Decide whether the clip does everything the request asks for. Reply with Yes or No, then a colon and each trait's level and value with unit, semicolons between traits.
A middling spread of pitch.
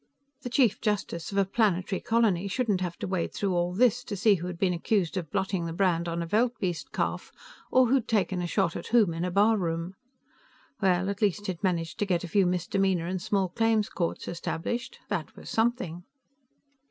Yes: average, 3.5 semitones